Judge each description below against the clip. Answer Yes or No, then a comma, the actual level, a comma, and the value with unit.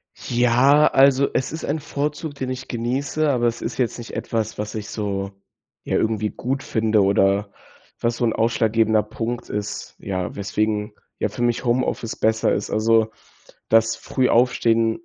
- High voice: No, low, 115 Hz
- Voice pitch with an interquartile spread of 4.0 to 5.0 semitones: No, average, 2.9 semitones